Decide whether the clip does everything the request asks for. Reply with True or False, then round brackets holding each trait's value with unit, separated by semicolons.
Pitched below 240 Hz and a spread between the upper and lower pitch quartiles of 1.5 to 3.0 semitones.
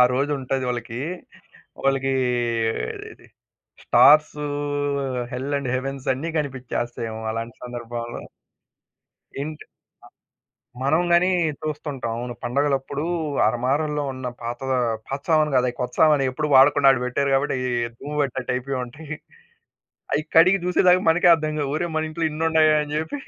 False (140 Hz; 3.5 semitones)